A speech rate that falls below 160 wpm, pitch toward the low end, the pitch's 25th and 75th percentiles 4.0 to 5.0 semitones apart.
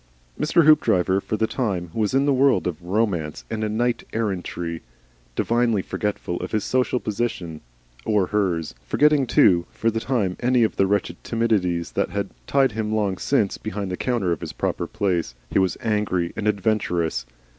No: average, 170 wpm; low, 105 Hz; average, 4.4 semitones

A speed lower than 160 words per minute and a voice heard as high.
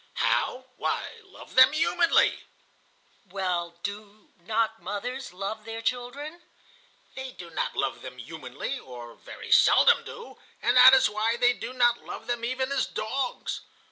Yes: average, 145 wpm; high, 240 Hz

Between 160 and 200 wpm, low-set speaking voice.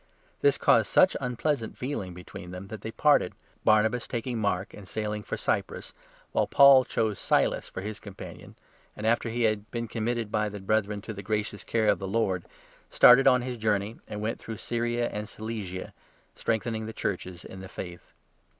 Yes: average, 185 wpm; low, 110 Hz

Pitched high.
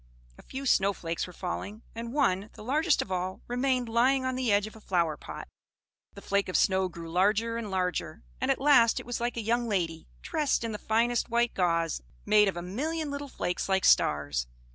Yes: high, 215 Hz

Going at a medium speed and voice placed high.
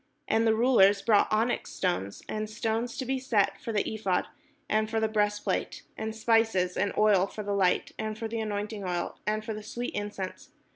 Yes: average, 195 wpm; high, 215 Hz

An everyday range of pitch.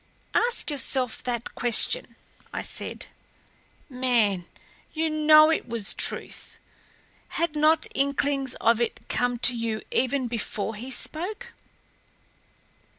Yes: average, 4.7 semitones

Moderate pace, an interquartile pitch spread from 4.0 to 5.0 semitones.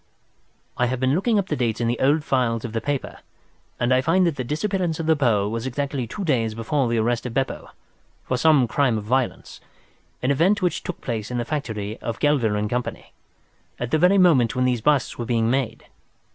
No: fast, 215 wpm; average, 4.5 semitones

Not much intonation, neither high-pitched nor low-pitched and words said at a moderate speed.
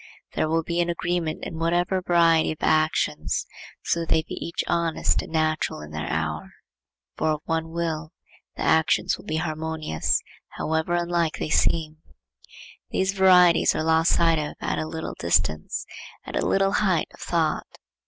Yes: narrow, 1.6 semitones; medium, 160 Hz; average, 165 wpm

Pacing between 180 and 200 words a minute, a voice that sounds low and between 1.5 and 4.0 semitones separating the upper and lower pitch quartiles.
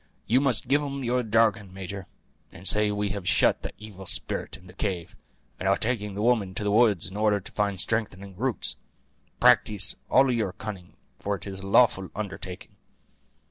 Yes: average, 190 wpm; low, 105 Hz; average, 2.8 semitones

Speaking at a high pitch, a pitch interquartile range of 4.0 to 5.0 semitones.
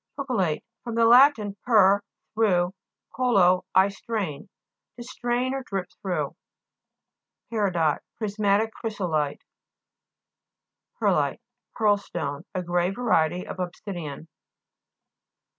Yes: high, 200 Hz; average, 4.5 semitones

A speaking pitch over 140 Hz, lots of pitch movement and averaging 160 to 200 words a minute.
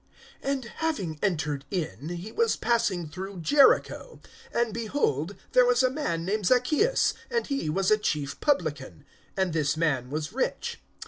No: high, 190 Hz; wide, 8.4 semitones; average, 150 wpm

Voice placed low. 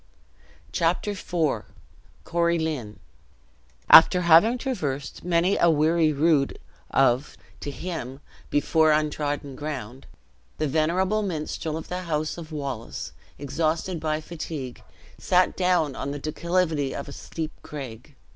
No: medium, 155 Hz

